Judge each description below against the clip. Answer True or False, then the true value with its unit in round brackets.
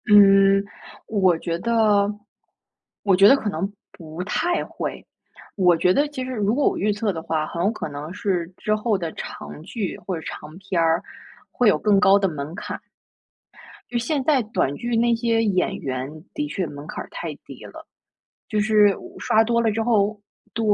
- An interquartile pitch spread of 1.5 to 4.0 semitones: False (4.7 semitones)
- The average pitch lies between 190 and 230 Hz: True (200 Hz)